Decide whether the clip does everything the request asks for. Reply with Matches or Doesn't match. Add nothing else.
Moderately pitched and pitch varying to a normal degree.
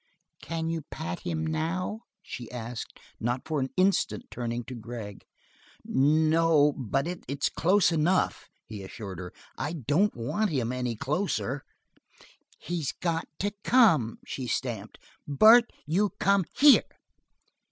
Doesn't match